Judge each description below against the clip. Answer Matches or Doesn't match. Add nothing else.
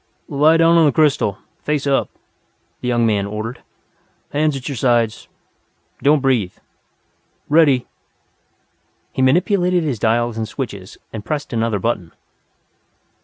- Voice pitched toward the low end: Matches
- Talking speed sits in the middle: Doesn't match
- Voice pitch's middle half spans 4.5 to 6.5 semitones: Matches